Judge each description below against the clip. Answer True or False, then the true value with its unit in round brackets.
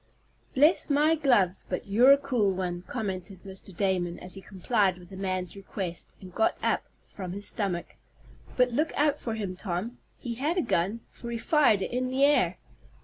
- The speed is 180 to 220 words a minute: True (190 wpm)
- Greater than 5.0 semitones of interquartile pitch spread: True (5.4 semitones)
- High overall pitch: True (205 Hz)